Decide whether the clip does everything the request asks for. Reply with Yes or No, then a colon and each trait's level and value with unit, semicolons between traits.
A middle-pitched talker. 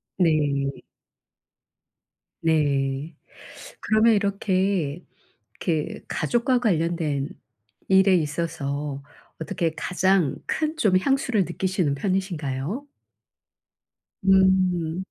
Yes: medium, 175 Hz